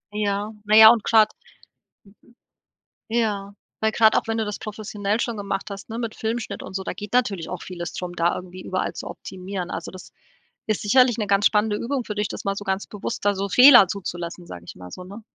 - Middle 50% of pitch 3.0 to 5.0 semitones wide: No, narrow, 2.6 semitones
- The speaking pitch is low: No, high, 205 Hz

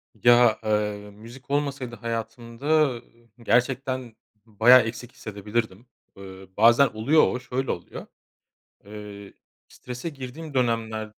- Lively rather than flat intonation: No, average, 2.9 semitones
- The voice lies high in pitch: No, low, 115 Hz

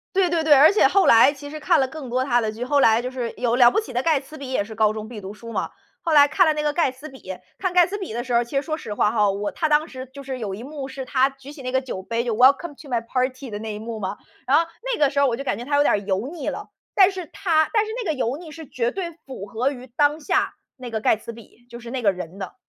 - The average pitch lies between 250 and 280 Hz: Yes, very high, 260 Hz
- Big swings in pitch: No, average, 4.7 semitones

